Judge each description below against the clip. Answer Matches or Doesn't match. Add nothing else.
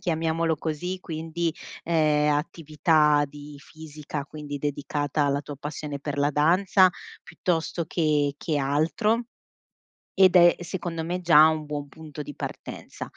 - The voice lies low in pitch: Doesn't match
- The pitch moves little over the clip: Matches